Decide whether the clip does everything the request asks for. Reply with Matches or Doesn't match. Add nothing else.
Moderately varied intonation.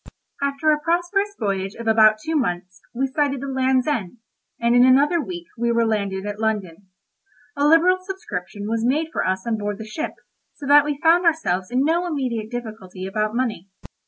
Doesn't match